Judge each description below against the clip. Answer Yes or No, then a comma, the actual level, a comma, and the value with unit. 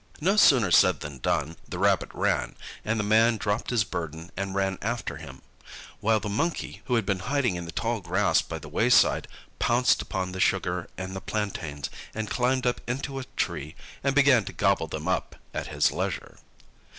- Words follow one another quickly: No, average, 190 wpm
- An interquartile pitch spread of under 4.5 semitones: No, average, 4.9 semitones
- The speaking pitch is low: Yes, low, 105 Hz